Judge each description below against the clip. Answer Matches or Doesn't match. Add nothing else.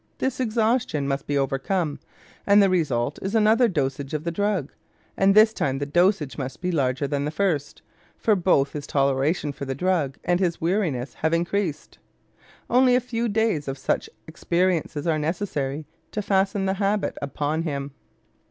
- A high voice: Doesn't match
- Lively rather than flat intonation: Matches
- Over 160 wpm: Matches